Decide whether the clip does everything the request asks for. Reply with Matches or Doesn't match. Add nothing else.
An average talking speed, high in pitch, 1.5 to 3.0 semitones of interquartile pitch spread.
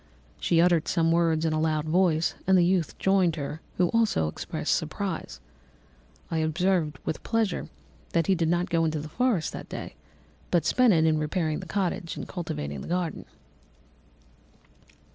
Doesn't match